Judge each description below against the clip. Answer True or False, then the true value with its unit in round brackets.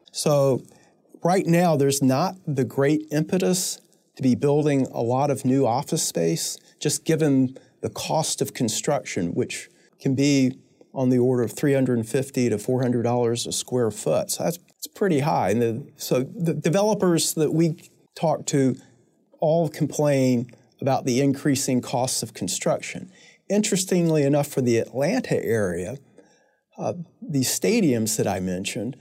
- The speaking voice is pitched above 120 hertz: True (140 Hz)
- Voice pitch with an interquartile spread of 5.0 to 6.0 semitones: False (4.5 semitones)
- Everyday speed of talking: True (145 wpm)